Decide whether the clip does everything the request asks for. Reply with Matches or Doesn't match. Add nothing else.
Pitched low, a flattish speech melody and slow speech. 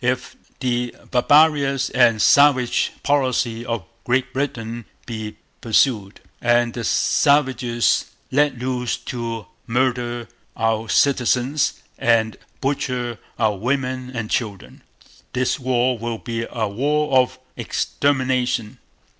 Matches